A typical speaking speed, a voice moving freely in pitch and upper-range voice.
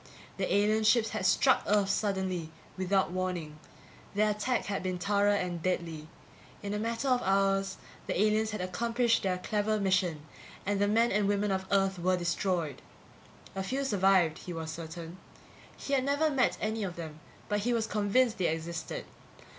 No: average, 170 wpm; average, 3.0 semitones; high, 195 Hz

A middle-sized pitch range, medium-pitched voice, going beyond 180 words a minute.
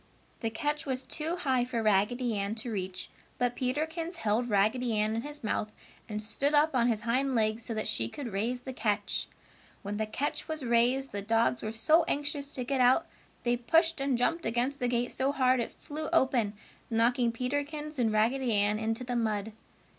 No: average, 3.9 semitones; high, 245 Hz; average, 195 wpm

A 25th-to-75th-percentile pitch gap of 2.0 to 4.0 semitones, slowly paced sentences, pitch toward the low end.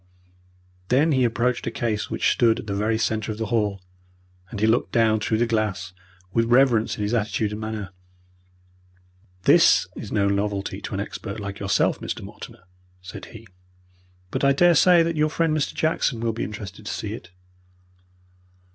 No: average, 2.9 semitones; average, 175 wpm; low, 110 Hz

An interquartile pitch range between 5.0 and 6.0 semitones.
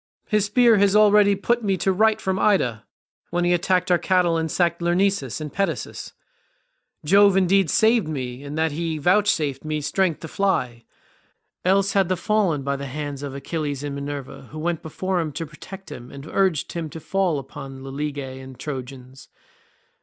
Yes: wide, 5.4 semitones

